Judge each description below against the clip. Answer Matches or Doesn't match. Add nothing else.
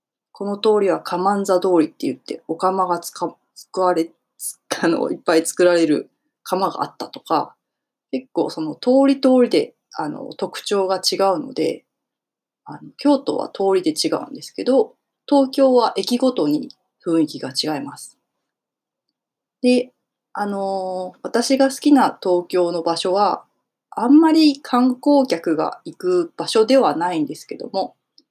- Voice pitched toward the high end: Matches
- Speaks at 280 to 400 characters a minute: Doesn't match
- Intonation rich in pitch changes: Matches